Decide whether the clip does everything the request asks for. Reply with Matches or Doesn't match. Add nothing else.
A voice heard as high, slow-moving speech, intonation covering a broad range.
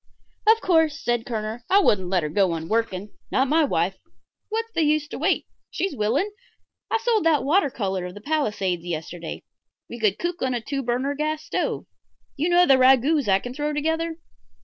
Doesn't match